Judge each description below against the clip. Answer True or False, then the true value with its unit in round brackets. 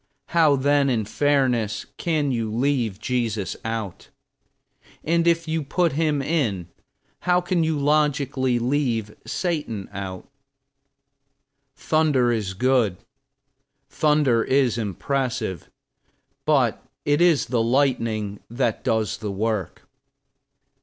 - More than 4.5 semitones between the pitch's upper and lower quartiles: True (5.1 semitones)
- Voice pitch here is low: True (130 Hz)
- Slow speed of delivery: True (105 wpm)